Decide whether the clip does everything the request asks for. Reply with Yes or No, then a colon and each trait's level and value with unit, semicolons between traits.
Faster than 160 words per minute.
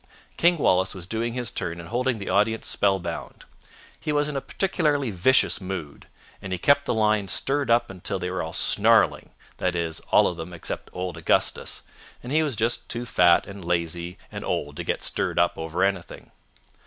Yes: average, 190 wpm